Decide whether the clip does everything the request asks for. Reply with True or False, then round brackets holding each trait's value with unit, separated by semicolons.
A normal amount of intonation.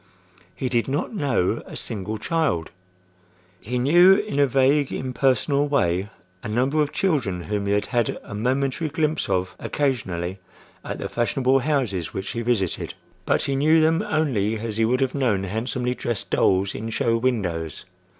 False (6.1 semitones)